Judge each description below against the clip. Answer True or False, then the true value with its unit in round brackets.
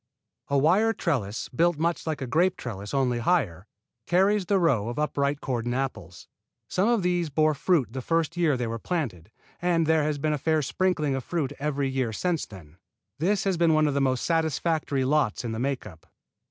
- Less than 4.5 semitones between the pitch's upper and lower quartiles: False (5.2 semitones)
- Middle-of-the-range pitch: True (150 Hz)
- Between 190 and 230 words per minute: True (200 wpm)